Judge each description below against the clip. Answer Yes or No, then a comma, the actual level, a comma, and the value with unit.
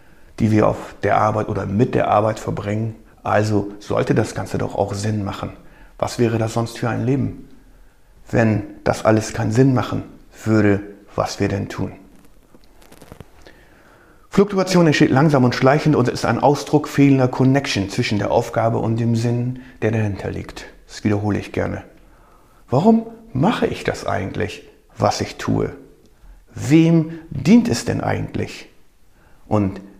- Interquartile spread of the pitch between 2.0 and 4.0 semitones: No, average, 4.5 semitones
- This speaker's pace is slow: No, average, 150 wpm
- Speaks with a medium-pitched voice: No, low, 115 Hz